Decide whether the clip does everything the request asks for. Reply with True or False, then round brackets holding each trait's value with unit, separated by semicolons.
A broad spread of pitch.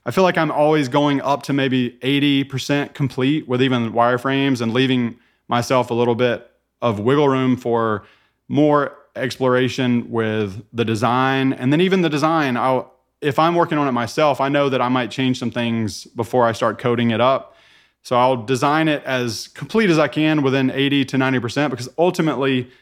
False (2.9 semitones)